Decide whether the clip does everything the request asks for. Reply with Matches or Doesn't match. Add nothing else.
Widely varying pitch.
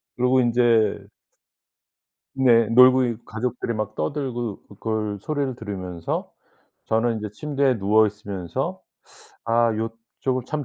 Doesn't match